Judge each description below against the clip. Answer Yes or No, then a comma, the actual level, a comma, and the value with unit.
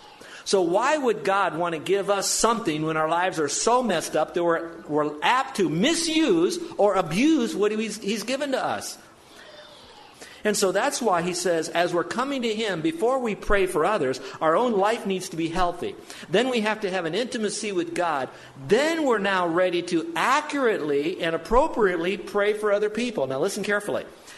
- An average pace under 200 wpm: Yes, average, 190 wpm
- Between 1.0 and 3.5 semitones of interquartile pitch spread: No, wide, 5.5 semitones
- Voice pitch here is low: No, high, 200 Hz